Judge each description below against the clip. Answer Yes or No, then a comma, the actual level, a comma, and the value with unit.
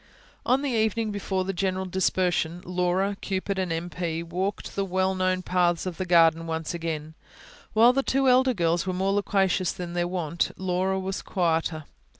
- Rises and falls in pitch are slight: Yes, narrow, 2.1 semitones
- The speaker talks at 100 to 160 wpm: No, average, 175 wpm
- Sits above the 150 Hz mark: Yes, medium, 185 Hz